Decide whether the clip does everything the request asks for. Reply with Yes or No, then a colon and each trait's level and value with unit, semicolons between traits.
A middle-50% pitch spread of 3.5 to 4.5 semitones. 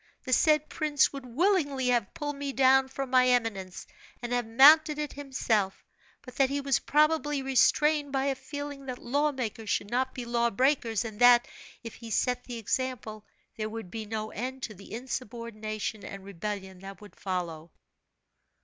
Yes: average, 4.2 semitones